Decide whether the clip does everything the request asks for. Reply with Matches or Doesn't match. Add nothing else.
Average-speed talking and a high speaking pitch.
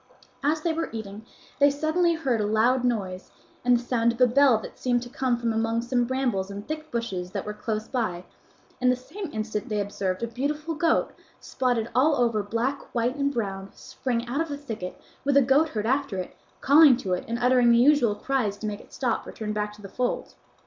Doesn't match